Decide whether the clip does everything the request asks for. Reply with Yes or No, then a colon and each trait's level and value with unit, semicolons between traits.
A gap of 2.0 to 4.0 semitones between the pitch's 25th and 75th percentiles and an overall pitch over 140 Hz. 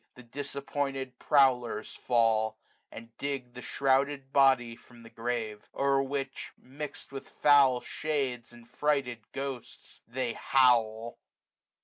No: average, 2.7 semitones; low, 130 Hz